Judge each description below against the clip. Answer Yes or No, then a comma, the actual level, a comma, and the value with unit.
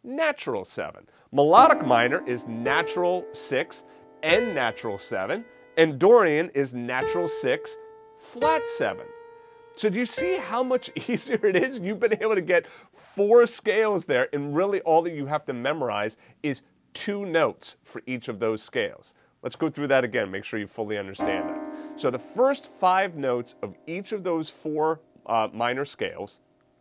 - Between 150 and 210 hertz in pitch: Yes, medium, 185 Hz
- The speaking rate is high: No, average, 165 wpm